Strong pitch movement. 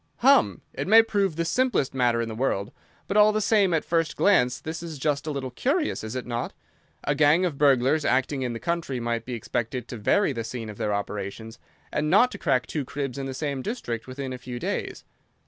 Yes: wide, 5.7 semitones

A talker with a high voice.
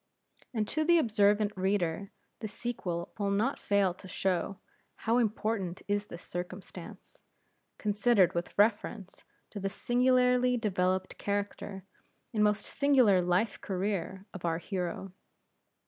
Yes: high, 205 Hz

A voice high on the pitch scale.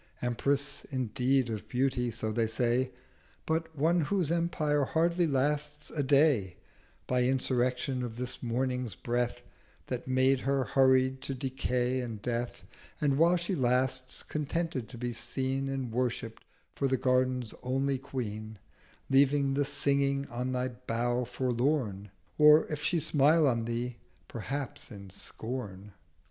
No: low, 130 Hz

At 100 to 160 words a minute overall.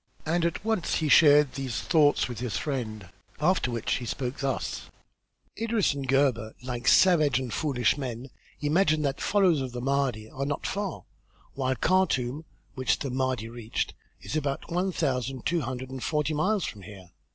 No: average, 170 wpm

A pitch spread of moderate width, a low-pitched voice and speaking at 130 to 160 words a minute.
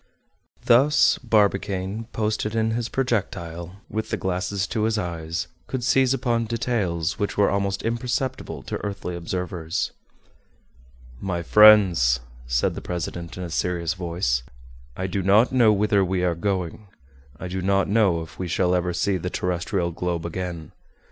Yes: average, 3.7 semitones; very low, 95 Hz; average, 150 wpm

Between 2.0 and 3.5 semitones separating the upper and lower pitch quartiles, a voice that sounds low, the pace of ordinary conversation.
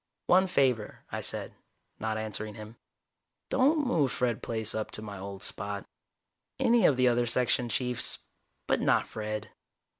Yes: average, 3.1 semitones; low, 115 Hz; average, 150 wpm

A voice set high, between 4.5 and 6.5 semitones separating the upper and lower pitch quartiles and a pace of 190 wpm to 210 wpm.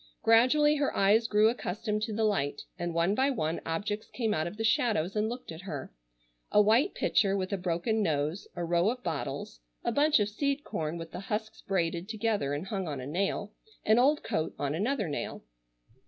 Yes: high, 205 Hz; average, 5.0 semitones; average, 200 wpm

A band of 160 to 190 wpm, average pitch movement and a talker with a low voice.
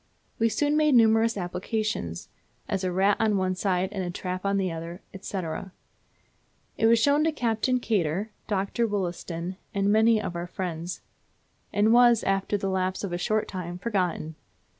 No: average, 165 wpm; average, 3.6 semitones; high, 195 Hz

